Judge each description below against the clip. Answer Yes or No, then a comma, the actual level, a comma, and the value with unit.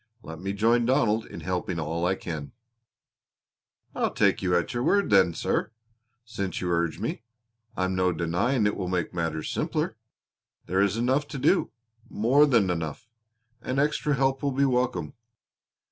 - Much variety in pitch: Yes, wide, 6.2 semitones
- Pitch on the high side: No, low, 100 Hz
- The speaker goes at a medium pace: Yes, average, 160 wpm